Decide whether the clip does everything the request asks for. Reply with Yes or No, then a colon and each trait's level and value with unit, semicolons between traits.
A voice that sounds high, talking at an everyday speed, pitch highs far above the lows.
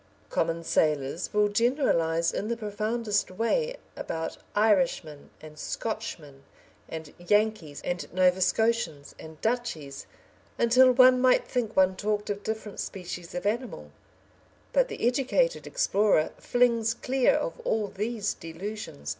No: high, 210 Hz; slow, 125 wpm; wide, 5.8 semitones